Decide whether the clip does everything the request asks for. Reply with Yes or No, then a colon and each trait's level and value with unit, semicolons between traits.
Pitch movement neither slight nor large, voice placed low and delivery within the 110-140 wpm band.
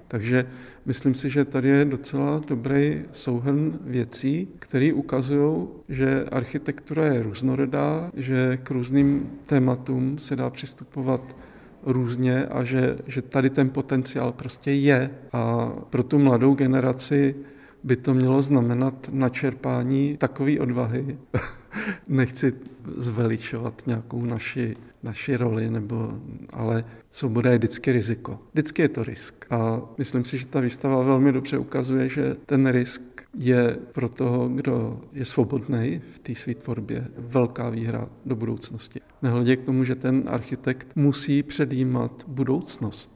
No: narrow, 2.2 semitones; low, 130 Hz; average, 130 wpm